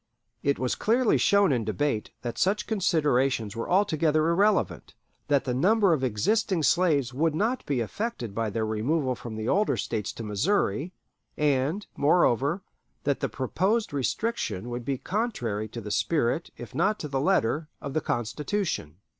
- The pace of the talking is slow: No, average, 160 wpm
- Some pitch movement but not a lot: No, wide, 8.1 semitones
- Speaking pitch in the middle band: Yes, medium, 145 Hz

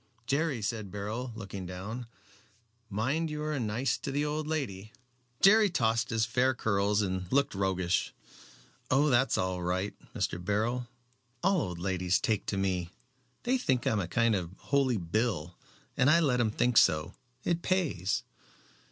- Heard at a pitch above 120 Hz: No, low, 115 Hz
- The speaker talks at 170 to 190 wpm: No, average, 155 wpm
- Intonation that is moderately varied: No, wide, 6.1 semitones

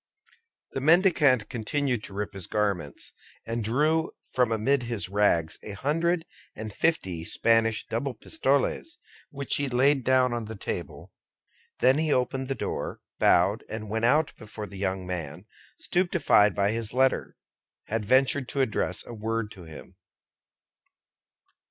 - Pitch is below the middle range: Yes, low, 115 Hz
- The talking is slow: No, average, 145 wpm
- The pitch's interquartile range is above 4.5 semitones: Yes, average, 5.0 semitones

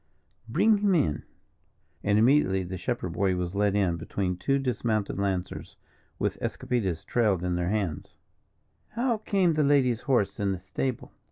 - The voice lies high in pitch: No, low, 105 Hz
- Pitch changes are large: Yes, wide, 6.7 semitones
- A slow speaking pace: No, average, 155 wpm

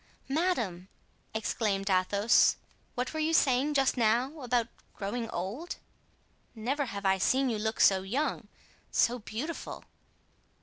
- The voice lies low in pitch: No, high, 235 Hz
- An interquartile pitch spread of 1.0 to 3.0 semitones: No, average, 5.2 semitones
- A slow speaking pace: Yes, slow, 125 wpm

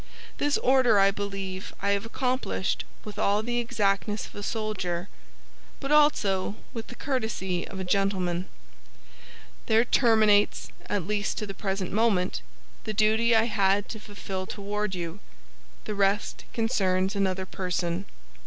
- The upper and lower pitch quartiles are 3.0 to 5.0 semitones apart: No, narrow, 2.6 semitones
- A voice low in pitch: No, high, 205 Hz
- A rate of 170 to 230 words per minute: No, average, 140 wpm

